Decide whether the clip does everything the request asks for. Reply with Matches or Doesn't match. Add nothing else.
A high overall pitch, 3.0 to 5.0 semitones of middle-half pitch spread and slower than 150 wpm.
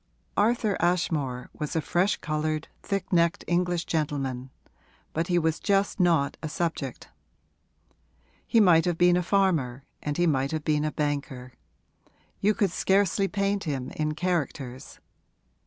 Doesn't match